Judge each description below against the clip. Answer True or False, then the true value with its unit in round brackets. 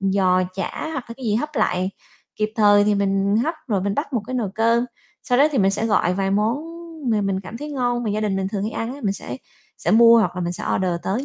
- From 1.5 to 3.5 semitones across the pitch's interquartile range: True (3.2 semitones)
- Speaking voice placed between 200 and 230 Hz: True (210 Hz)